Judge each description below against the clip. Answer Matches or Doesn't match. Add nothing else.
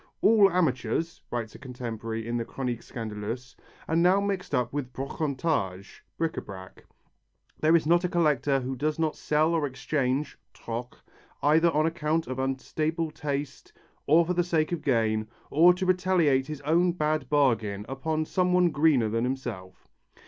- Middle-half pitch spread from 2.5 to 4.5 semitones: Doesn't match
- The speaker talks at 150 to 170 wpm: Matches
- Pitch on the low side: Doesn't match